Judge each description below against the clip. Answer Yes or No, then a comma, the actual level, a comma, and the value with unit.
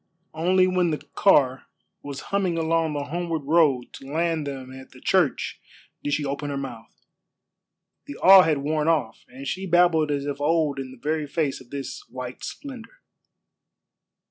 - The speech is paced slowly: No, average, 170 wpm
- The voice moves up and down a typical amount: Yes, average, 3.5 semitones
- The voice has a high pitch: No, medium, 150 Hz